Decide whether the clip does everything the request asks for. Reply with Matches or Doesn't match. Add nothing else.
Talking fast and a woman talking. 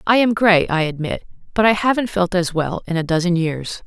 Matches